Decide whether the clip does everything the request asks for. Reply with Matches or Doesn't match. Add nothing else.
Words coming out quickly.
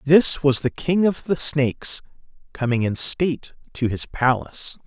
Doesn't match